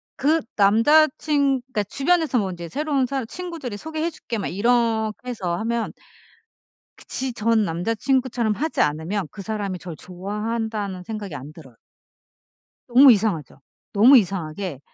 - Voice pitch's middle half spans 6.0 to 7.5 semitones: No, wide, 5.5 semitones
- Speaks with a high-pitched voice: Yes, high, 220 Hz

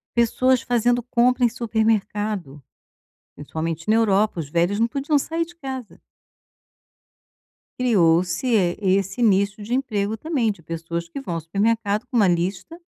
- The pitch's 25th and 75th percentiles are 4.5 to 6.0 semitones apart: Yes, wide, 5.4 semitones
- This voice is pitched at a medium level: No, high, 215 Hz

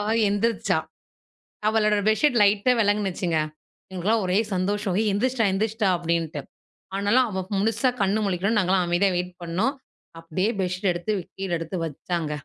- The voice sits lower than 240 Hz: Yes, high, 195 Hz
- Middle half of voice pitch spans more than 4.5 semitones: No, average, 3.2 semitones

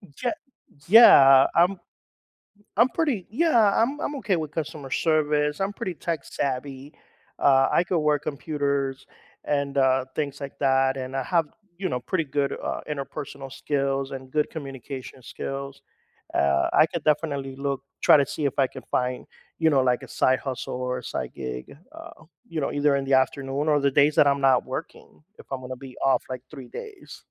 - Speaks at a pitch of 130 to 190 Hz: Yes, medium, 140 Hz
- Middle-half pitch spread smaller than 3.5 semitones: Yes, average, 2.9 semitones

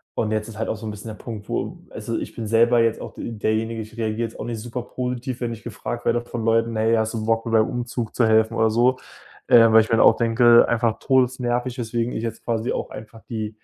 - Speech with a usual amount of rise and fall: No, narrow, 1.3 semitones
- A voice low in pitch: Yes, low, 115 Hz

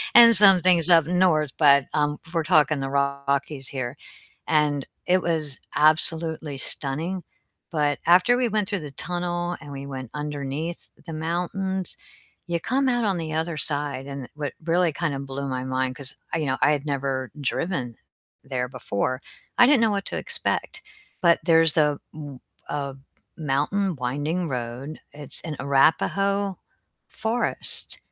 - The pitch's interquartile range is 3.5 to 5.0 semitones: Yes, average, 4.0 semitones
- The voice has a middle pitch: Yes, medium, 150 Hz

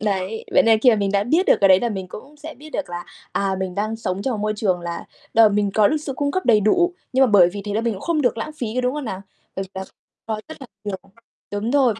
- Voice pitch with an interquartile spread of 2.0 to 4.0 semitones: No, average, 5.1 semitones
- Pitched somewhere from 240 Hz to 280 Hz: No, high, 215 Hz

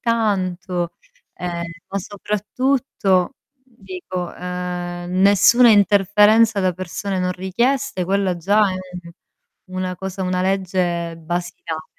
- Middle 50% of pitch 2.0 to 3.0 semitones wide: Yes, narrow, 2.5 semitones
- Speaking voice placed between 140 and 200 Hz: Yes, medium, 185 Hz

